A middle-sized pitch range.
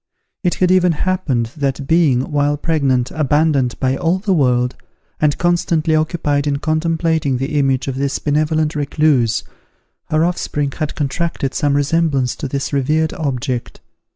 Yes: average, 3.0 semitones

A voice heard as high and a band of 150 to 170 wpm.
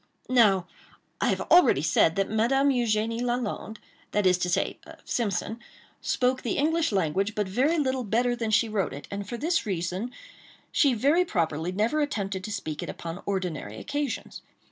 Yes: high, 215 Hz; average, 160 wpm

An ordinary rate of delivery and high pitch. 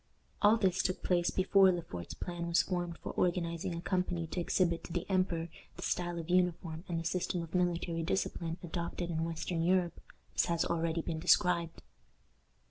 No: average, 180 wpm; medium, 170 Hz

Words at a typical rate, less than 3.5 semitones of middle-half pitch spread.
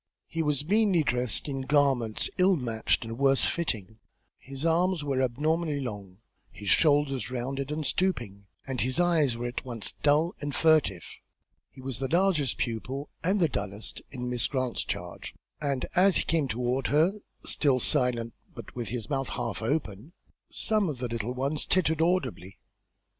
No: average, 165 wpm; average, 4.7 semitones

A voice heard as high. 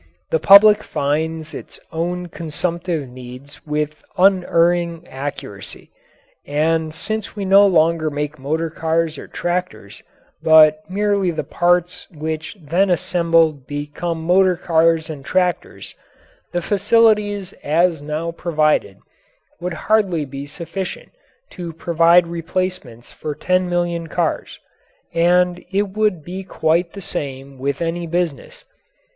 No: medium, 170 Hz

